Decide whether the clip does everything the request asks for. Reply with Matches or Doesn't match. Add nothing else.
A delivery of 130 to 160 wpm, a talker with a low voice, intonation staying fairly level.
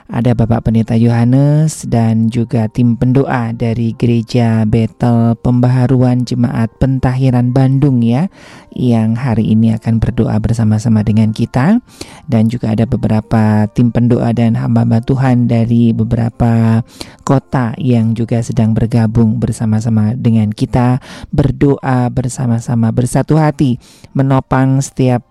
Doesn't match